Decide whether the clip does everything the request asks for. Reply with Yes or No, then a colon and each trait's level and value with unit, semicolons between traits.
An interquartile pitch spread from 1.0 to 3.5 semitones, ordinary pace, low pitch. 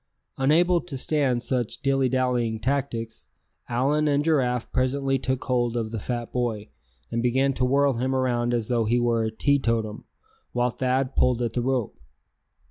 Yes: narrow, 2.4 semitones; average, 165 wpm; low, 125 Hz